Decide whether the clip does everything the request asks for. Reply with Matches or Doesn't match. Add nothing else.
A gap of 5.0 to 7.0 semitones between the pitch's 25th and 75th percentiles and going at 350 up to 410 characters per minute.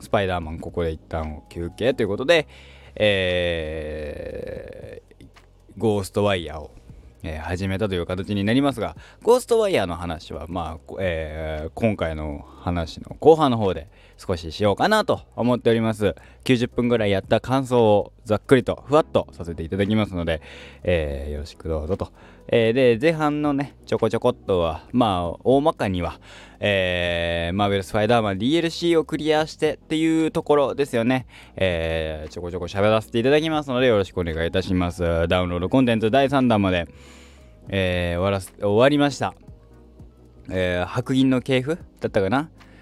Matches